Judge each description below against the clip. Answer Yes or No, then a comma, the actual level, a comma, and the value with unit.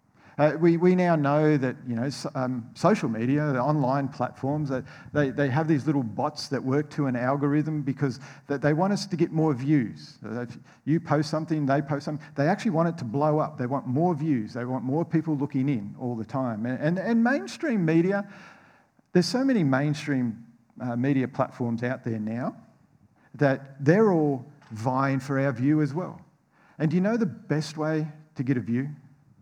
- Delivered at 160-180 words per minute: No, average, 200 wpm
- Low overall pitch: No, medium, 145 Hz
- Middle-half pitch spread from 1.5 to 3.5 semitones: Yes, average, 3.2 semitones